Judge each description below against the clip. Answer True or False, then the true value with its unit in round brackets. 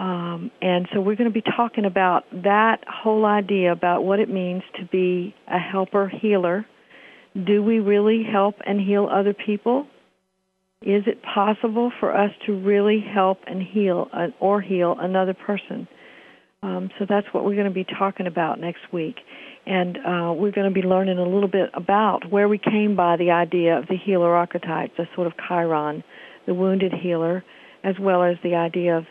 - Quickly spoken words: False (185 wpm)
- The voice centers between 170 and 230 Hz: True (190 Hz)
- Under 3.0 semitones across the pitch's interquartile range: True (2.4 semitones)